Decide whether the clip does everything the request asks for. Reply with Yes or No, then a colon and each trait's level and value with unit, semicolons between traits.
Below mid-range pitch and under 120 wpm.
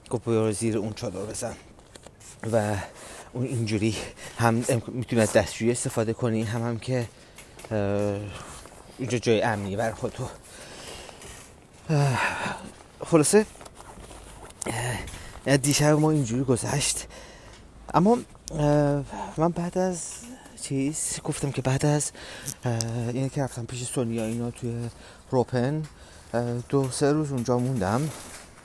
Yes: low, 125 Hz; slow, 105 wpm